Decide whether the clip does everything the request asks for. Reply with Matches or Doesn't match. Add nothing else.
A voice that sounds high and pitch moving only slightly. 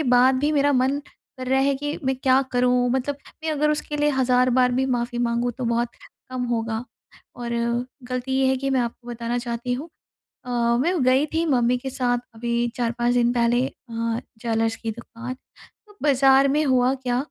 Matches